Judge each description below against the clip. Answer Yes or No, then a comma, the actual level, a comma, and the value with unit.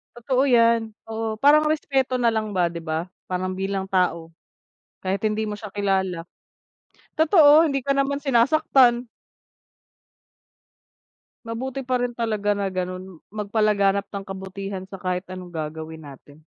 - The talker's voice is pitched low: No, high, 205 Hz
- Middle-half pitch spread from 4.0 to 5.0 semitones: Yes, average, 4.7 semitones